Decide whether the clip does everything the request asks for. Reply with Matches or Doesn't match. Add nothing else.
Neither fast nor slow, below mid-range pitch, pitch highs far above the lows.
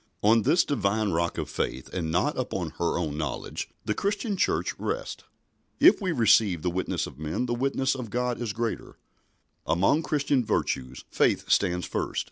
Matches